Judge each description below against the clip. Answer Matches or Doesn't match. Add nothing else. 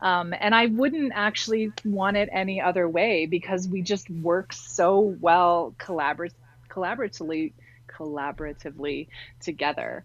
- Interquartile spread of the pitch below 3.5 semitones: Doesn't match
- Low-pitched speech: Doesn't match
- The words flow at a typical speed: Doesn't match